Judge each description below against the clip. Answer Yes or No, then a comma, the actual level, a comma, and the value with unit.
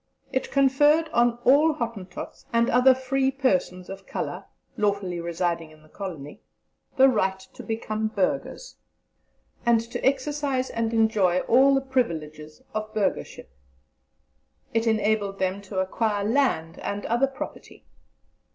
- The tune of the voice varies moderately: No, wide, 5.7 semitones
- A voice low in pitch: No, high, 220 Hz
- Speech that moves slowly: Yes, slow, 130 wpm